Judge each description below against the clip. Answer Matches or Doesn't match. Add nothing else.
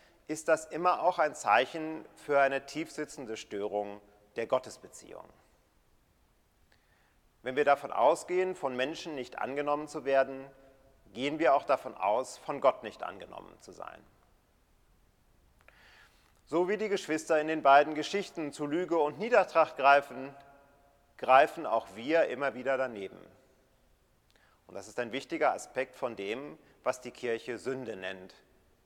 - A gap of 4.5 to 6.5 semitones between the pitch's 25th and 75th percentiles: Doesn't match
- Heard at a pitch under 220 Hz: Matches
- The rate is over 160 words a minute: Doesn't match